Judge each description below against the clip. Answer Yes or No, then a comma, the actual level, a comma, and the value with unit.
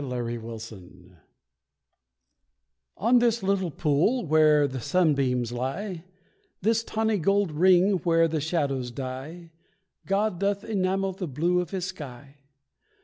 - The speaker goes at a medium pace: No, slow, 125 wpm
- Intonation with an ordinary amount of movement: No, wide, 6.5 semitones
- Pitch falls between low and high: Yes, medium, 165 Hz